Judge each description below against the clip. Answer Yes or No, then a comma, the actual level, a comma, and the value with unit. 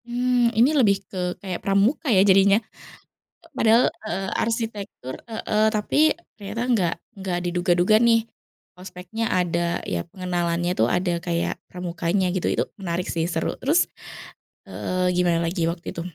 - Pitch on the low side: No, medium, 185 Hz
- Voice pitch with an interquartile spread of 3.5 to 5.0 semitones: Yes, average, 4.0 semitones